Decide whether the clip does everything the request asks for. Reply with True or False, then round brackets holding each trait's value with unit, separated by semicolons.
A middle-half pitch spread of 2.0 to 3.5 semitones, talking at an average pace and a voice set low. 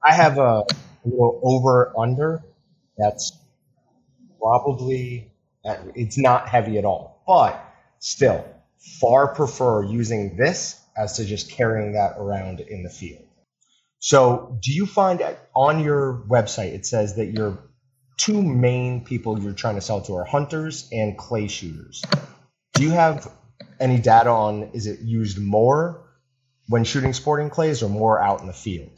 False (3.9 semitones; 150 wpm; 120 Hz)